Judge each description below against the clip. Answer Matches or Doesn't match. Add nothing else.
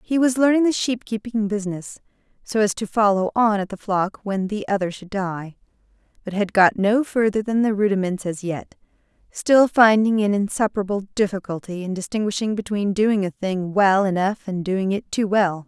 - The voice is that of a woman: Matches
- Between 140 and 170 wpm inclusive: Doesn't match